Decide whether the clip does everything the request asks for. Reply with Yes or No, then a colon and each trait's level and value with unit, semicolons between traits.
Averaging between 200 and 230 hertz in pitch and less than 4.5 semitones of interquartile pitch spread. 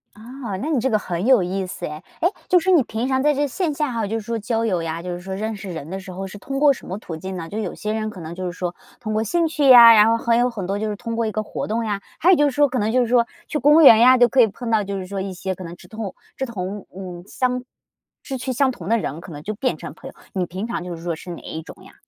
No: high, 215 Hz; average, 5.1 semitones